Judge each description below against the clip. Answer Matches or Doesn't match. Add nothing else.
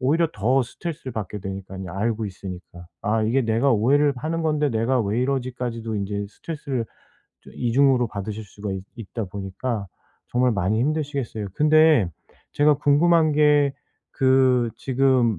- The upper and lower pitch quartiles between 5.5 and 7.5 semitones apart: Doesn't match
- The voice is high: Doesn't match